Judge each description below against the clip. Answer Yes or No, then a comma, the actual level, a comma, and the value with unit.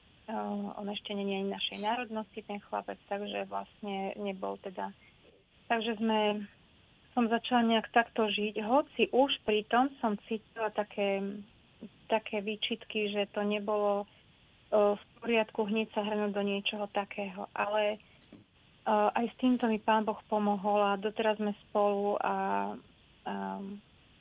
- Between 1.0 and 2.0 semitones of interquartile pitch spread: Yes, narrow, 1.5 semitones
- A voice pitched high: Yes, high, 210 Hz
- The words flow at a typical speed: Yes, average, 135 wpm